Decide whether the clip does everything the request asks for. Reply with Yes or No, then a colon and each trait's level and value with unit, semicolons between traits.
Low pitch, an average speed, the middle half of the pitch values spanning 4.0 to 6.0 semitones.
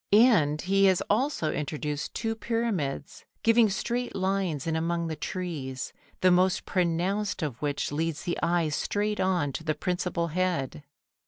No: medium, 175 Hz; average, 150 wpm; average, 4.4 semitones